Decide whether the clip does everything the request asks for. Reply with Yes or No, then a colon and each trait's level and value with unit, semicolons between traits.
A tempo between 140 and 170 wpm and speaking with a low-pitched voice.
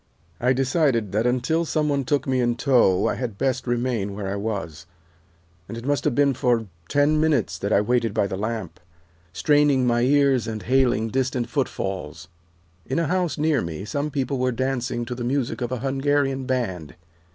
No: average, 185 wpm; low, 125 Hz